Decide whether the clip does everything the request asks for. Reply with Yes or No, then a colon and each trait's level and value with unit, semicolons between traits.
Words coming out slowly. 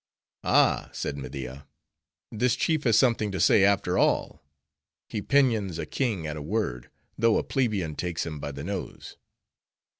No: average, 155 wpm